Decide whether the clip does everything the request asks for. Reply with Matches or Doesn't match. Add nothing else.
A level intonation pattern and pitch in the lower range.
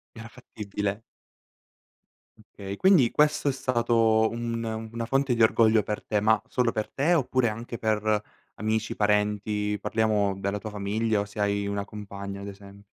Matches